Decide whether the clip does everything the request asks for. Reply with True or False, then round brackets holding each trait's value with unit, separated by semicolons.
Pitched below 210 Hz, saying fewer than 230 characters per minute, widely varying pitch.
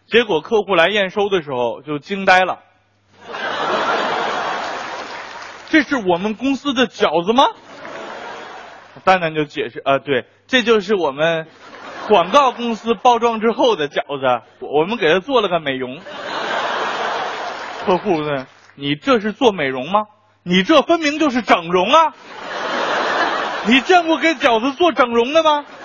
False (220 Hz; 200 characters per minute; 8.7 semitones)